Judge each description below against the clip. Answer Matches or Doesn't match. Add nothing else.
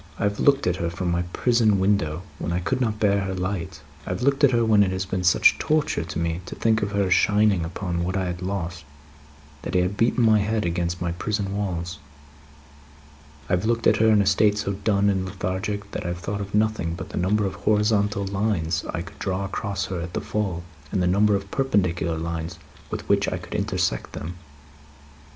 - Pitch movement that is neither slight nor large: Matches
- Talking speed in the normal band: Doesn't match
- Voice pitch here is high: Doesn't match